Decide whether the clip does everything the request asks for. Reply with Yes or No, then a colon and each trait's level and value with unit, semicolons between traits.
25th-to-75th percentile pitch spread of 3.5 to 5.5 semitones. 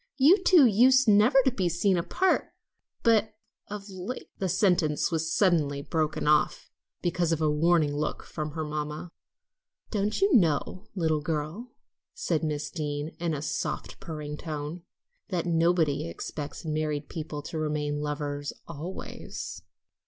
Yes: average, 4.1 semitones